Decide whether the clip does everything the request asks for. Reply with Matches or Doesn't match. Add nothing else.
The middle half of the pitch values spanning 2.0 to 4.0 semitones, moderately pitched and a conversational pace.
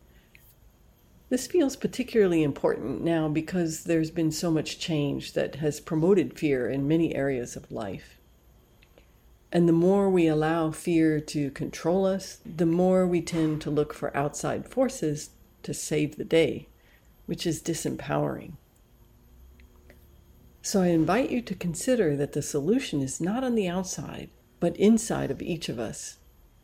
Matches